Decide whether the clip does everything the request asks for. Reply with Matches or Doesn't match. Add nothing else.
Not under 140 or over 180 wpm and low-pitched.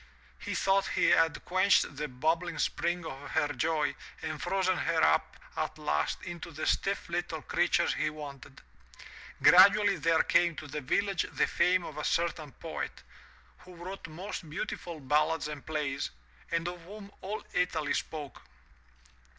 Doesn't match